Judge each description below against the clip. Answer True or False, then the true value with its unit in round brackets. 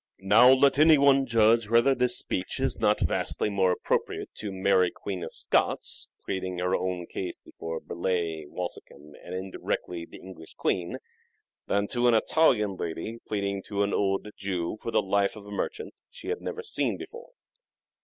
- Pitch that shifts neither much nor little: True (4.4 semitones)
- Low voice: True (100 Hz)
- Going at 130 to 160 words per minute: False (170 wpm)